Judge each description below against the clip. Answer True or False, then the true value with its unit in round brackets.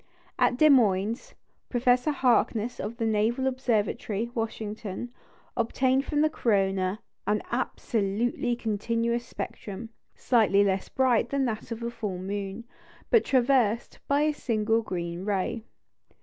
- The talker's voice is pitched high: True (230 Hz)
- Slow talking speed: True (125 wpm)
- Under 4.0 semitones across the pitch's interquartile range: True (3.1 semitones)